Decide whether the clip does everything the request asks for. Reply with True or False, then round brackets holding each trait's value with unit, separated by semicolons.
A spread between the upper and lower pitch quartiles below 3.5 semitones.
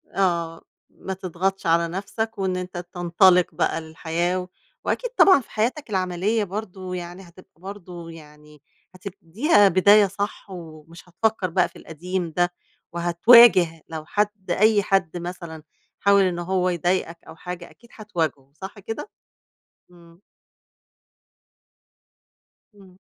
True (2.7 semitones)